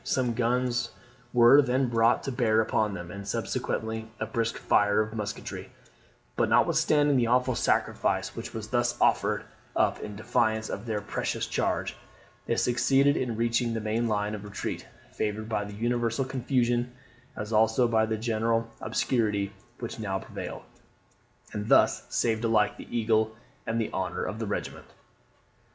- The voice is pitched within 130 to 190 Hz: No, low, 115 Hz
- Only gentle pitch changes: Yes, narrow, 2.0 semitones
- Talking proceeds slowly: No, average, 155 wpm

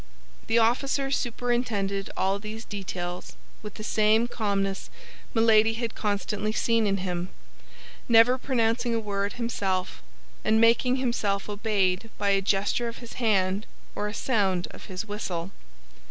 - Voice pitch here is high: Yes, high, 215 Hz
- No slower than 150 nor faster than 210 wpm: No, average, 140 wpm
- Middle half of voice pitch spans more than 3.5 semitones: No, average, 2.8 semitones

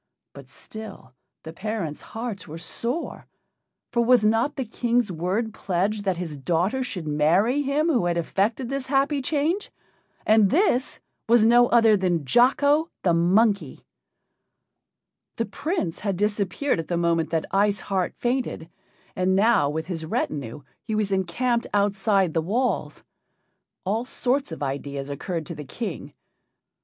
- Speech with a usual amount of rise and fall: No, wide, 6.1 semitones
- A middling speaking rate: Yes, average, 145 wpm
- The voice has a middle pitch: No, high, 205 Hz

